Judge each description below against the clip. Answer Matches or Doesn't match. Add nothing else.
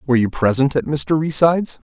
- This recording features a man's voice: Matches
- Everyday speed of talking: Matches